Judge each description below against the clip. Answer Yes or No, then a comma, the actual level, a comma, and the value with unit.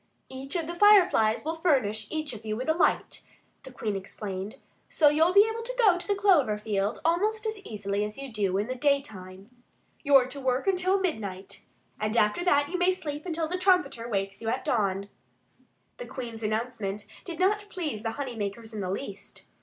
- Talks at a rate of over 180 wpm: Yes, average, 195 wpm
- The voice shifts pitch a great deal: Yes, wide, 8.8 semitones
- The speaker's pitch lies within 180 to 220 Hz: No, very high, 260 Hz